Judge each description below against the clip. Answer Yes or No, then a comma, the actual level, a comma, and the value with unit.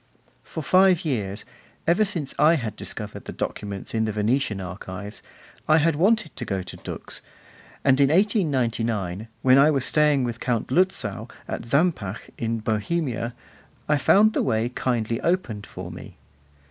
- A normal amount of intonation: No, wide, 6.5 semitones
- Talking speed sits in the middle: Yes, average, 155 wpm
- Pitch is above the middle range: No, low, 125 Hz